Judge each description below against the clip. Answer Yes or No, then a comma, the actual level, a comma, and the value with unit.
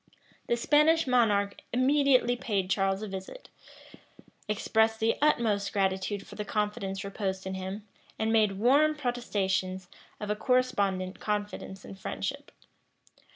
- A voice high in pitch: Yes, high, 210 Hz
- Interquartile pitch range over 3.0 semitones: Yes, average, 3.9 semitones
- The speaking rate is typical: No, slow, 125 wpm